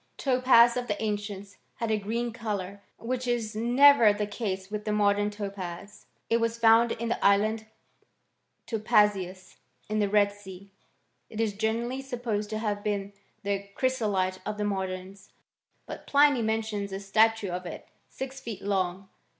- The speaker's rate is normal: Yes, average, 155 wpm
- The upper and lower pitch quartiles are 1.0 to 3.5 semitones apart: Yes, narrow, 2.5 semitones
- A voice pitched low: No, high, 210 Hz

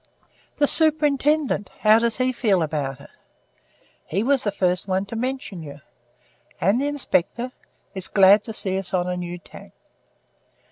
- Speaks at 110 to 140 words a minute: No, average, 155 wpm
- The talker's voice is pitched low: No, high, 205 Hz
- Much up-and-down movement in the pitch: Yes, wide, 6.1 semitones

